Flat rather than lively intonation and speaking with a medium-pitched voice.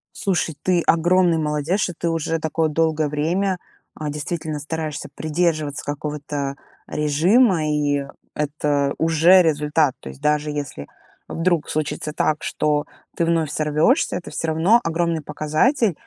Yes: narrow, 2.2 semitones; medium, 155 Hz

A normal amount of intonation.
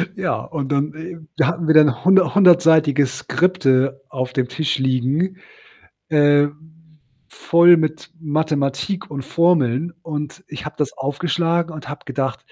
Yes: average, 3.6 semitones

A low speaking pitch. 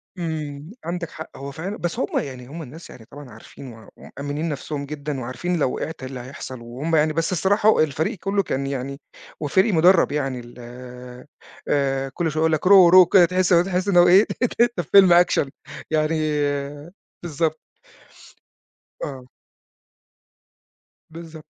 No: medium, 155 Hz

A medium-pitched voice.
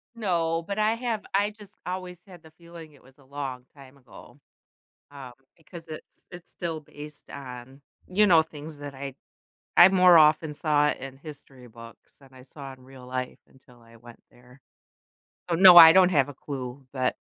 Yes: medium, 150 Hz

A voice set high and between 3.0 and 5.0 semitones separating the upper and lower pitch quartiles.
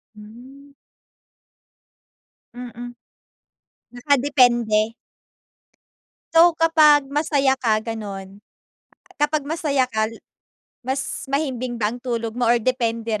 Yes: high, 245 Hz; average, 3.8 semitones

